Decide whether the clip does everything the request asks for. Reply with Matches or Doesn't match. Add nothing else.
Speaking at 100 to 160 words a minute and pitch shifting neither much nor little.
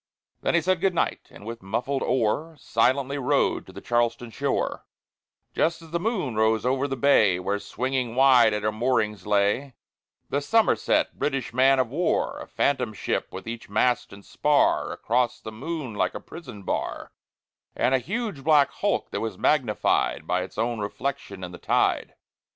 Doesn't match